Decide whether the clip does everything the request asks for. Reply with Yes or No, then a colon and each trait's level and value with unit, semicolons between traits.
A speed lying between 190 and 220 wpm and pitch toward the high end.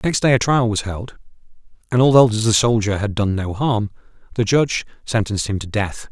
No: average, 195 wpm; low, 110 Hz